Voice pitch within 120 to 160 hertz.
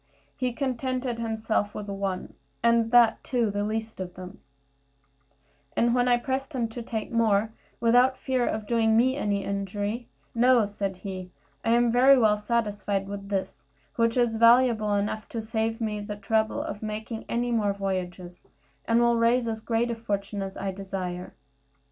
No: high, 220 Hz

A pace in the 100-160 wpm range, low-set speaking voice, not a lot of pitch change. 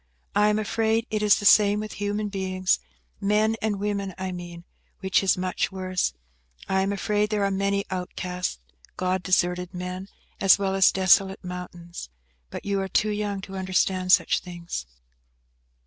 No: average, 155 wpm; high, 190 Hz; narrow, 2.0 semitones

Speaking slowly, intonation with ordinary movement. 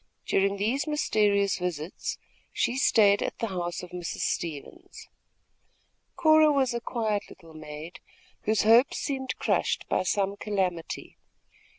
Yes: slow, 125 wpm; average, 5.0 semitones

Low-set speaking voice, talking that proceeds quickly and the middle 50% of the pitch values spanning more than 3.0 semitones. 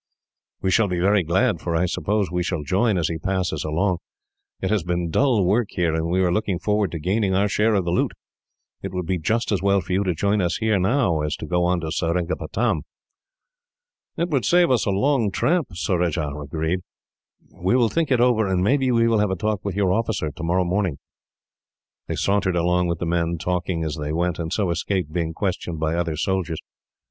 Yes: very low, 90 Hz; fast, 215 wpm; average, 3.5 semitones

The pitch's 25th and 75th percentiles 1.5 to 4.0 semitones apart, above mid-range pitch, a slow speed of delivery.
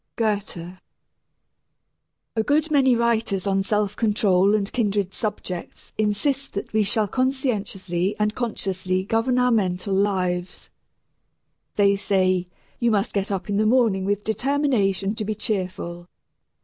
Yes: average, 2.9 semitones; high, 205 Hz; slow, 130 wpm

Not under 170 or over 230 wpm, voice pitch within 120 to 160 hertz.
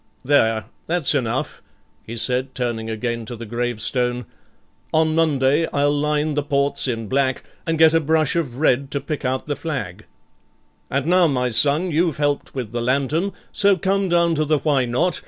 Yes: average, 175 wpm; medium, 140 Hz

